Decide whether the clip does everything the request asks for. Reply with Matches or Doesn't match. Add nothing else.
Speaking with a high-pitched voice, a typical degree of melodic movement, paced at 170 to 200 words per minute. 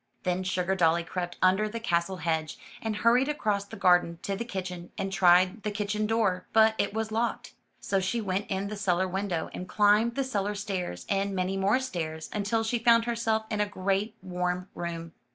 Matches